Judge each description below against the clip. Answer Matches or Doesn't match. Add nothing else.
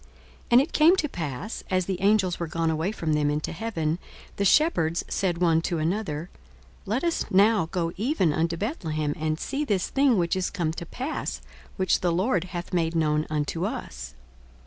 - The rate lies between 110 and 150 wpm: Doesn't match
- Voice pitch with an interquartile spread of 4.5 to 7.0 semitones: Matches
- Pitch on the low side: Doesn't match